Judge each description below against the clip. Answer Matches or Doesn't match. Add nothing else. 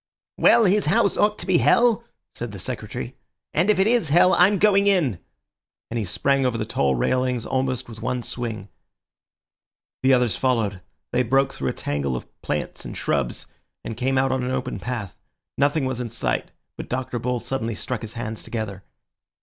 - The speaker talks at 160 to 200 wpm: Matches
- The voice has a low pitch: Matches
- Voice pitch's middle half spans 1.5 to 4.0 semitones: Doesn't match